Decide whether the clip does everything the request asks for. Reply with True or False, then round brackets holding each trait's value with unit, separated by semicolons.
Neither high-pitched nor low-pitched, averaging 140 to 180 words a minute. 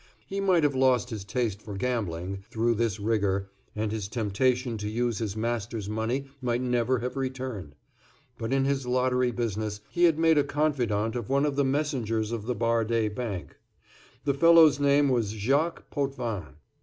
False (120 Hz; 170 wpm)